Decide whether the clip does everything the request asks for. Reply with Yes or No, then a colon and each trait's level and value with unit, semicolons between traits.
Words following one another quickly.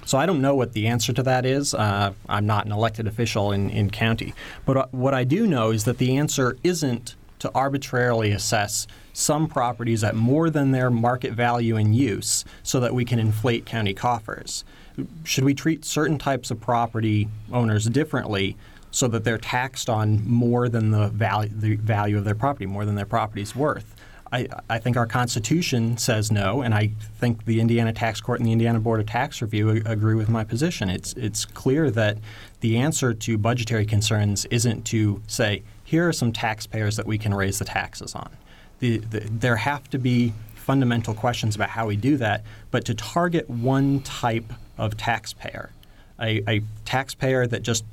No: average, 185 wpm